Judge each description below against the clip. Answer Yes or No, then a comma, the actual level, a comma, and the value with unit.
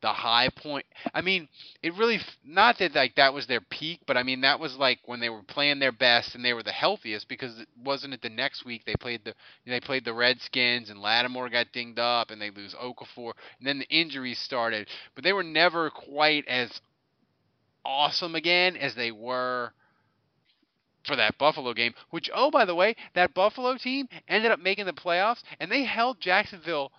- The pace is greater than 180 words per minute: Yes, average, 200 wpm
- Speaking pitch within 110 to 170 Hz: Yes, low, 135 Hz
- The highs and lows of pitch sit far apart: Yes, wide, 5.9 semitones